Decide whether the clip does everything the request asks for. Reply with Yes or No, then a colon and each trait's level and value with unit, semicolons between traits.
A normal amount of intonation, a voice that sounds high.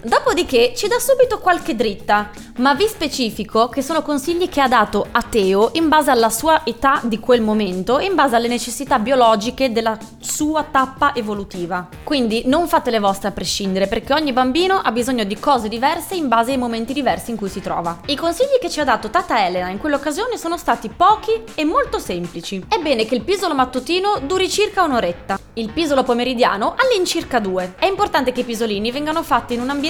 No: wide, 6.5 semitones; very high, 265 Hz